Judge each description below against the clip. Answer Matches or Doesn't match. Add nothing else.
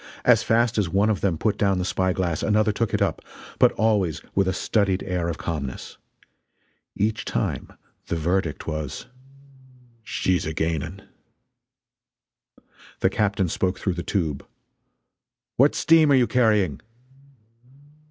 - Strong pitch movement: Doesn't match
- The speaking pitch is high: Doesn't match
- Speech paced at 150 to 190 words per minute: Doesn't match